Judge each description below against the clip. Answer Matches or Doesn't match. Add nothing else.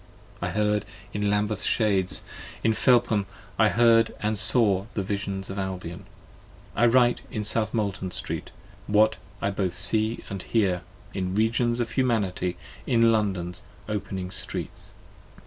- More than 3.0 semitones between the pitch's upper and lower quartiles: Doesn't match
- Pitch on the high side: Doesn't match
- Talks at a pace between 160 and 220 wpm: Doesn't match